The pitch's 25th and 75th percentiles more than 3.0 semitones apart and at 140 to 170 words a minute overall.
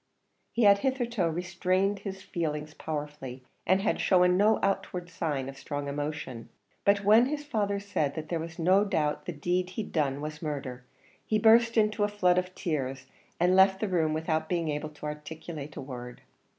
No: average, 5.0 semitones; average, 180 wpm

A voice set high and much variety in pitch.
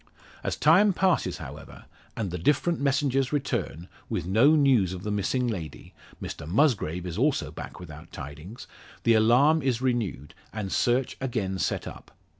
No: low, 115 Hz; wide, 7.1 semitones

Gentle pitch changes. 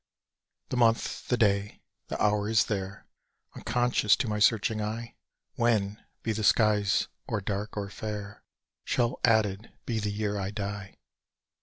Yes: narrow, 1.8 semitones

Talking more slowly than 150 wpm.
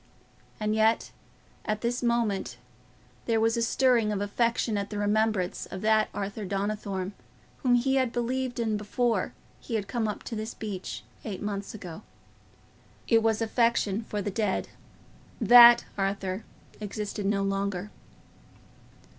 Yes: average, 140 wpm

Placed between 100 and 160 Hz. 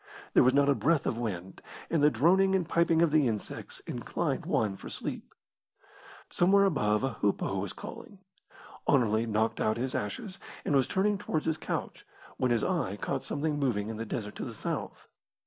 Yes: low, 135 Hz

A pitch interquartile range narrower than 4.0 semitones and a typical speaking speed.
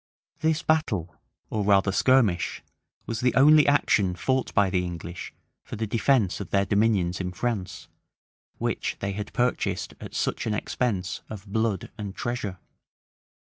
No: average, 4.5 semitones; average, 150 wpm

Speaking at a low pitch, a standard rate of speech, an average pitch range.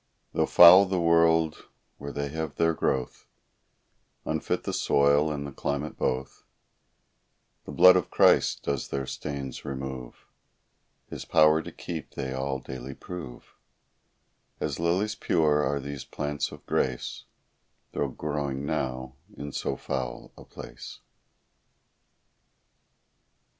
No: very low, 70 Hz; slow, 120 wpm; average, 3.1 semitones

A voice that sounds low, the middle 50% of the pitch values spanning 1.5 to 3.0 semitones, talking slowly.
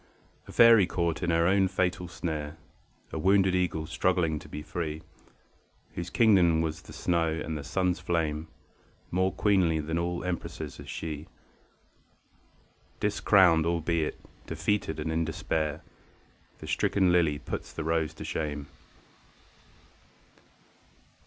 Yes: very low, 85 Hz; narrow, 2.5 semitones; slow, 125 wpm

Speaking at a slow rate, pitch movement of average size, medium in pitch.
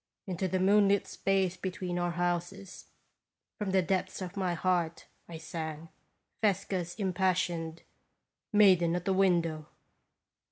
No: slow, 130 wpm; narrow, 2.1 semitones; medium, 180 Hz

